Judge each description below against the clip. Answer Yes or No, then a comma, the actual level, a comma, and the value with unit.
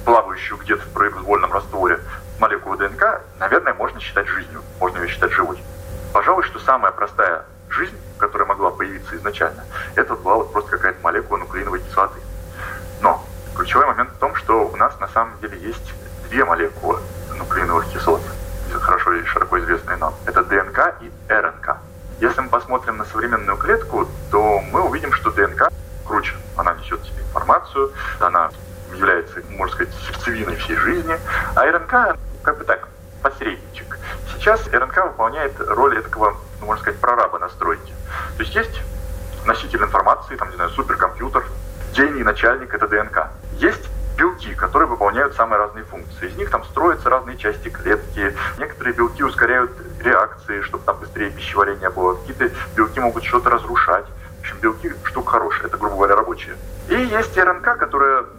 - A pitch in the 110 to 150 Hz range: No, very low, 90 Hz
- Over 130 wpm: Yes, average, 155 wpm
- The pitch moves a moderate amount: Yes, average, 3.7 semitones